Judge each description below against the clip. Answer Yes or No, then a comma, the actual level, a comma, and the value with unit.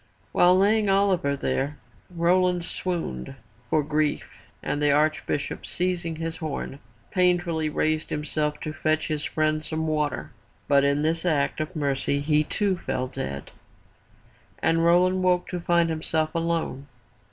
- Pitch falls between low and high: Yes, medium, 155 Hz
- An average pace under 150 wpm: Yes, average, 140 wpm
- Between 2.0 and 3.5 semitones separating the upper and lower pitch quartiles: Yes, average, 2.9 semitones